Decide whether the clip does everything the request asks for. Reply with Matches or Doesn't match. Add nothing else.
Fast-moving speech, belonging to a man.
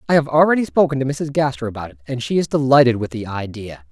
Matches